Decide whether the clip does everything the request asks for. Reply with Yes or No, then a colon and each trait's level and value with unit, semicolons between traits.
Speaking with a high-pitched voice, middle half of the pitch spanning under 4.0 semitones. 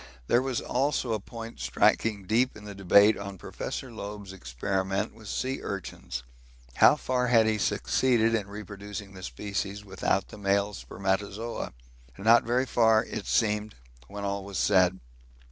No: low, 105 Hz; narrow, 2.6 semitones